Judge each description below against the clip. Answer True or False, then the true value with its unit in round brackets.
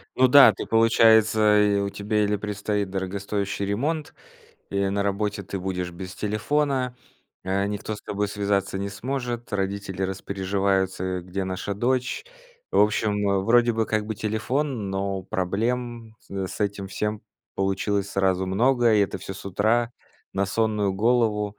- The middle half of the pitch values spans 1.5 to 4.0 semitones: True (2.4 semitones)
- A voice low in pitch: True (100 Hz)